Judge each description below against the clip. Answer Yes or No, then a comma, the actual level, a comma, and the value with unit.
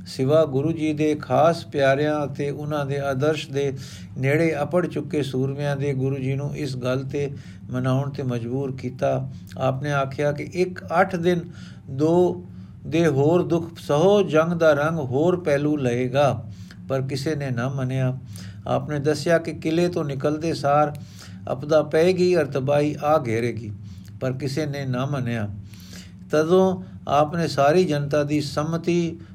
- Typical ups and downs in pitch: Yes, average, 3.2 semitones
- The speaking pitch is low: No, medium, 145 Hz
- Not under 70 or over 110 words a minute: No, average, 145 wpm